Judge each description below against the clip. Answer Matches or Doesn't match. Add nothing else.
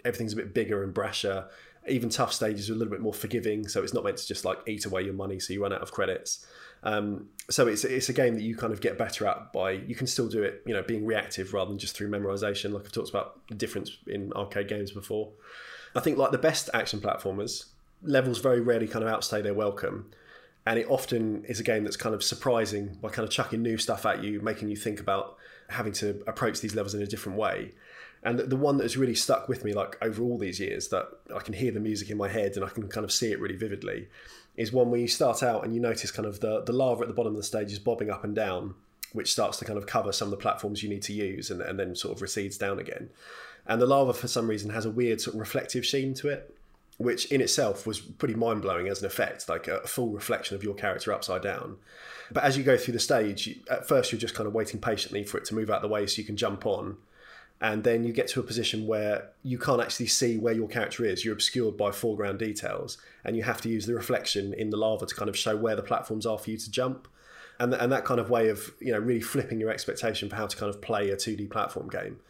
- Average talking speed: Doesn't match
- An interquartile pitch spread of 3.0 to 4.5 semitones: Doesn't match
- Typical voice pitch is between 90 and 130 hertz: Matches